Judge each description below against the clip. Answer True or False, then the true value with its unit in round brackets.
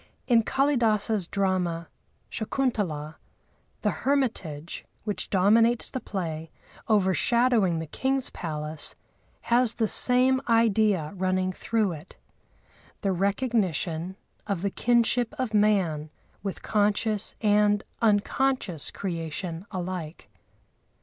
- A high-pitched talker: True (205 Hz)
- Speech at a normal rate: False (95 wpm)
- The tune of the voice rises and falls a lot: False (4.9 semitones)